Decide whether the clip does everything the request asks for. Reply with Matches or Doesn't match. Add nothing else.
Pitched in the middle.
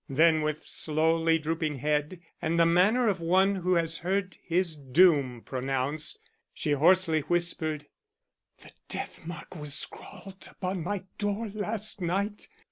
Matches